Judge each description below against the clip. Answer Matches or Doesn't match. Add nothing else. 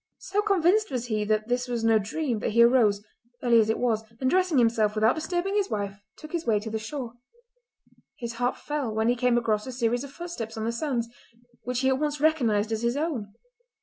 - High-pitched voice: Matches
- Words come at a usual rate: Doesn't match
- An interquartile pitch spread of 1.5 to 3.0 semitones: Doesn't match